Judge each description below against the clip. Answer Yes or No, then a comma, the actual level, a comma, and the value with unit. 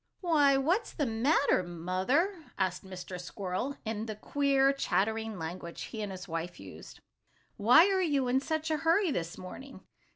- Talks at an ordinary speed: Yes, average, 160 wpm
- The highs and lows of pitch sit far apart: Yes, wide, 7.6 semitones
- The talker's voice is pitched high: Yes, high, 225 Hz